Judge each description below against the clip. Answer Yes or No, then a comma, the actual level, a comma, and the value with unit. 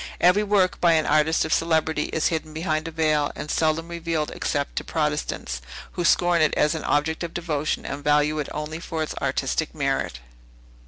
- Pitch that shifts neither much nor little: No, narrow, 1.7 semitones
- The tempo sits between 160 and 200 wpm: Yes, average, 190 wpm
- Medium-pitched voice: Yes, medium, 160 Hz